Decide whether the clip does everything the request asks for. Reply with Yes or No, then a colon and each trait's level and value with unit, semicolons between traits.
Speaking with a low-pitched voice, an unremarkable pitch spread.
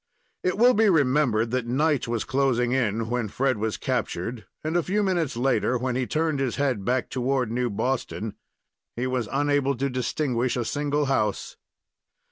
Yes: low, 130 Hz; average, 3.4 semitones